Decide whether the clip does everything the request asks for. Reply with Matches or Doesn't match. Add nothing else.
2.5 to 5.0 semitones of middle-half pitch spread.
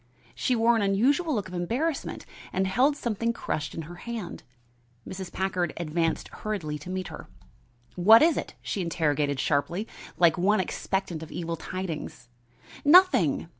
Doesn't match